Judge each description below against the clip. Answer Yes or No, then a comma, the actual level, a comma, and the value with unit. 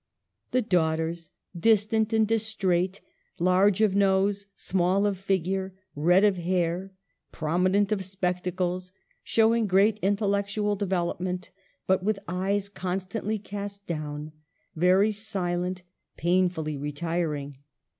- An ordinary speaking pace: No, slow, 110 wpm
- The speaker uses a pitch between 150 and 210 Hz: Yes, high, 190 Hz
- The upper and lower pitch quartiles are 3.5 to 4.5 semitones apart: No, narrow, 2.5 semitones